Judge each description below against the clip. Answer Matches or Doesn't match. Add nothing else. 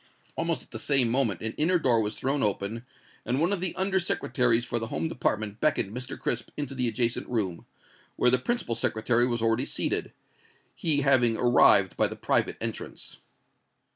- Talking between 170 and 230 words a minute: Matches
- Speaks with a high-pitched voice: Doesn't match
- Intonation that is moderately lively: Matches